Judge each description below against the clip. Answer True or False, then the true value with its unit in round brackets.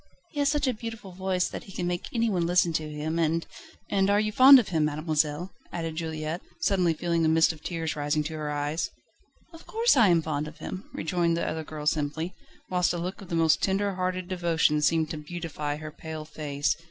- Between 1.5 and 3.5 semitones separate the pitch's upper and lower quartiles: True (3.1 semitones)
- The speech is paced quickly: True (220 wpm)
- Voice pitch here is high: False (165 Hz)